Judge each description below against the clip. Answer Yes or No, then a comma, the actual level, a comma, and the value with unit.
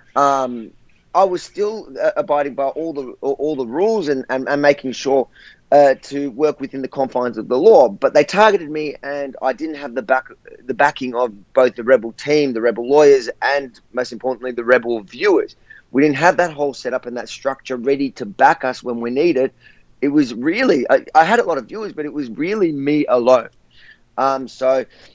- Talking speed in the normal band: No, fast, 210 wpm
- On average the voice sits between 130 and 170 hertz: Yes, medium, 140 Hz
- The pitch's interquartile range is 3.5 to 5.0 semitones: No, average, 2.9 semitones